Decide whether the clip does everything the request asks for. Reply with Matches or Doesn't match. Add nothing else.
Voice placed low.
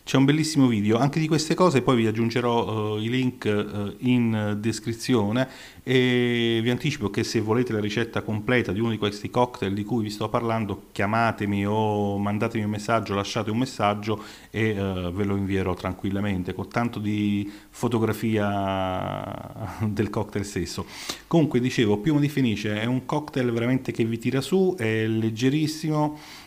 Matches